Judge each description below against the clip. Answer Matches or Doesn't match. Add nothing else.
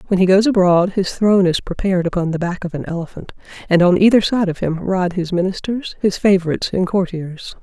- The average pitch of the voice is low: Doesn't match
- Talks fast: Matches